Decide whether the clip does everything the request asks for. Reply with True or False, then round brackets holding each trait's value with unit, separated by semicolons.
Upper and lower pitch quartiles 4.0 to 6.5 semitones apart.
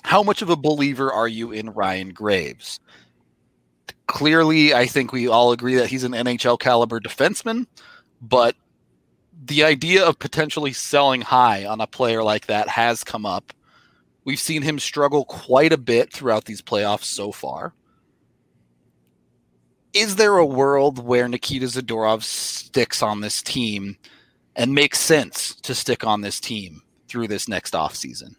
True (5.2 semitones)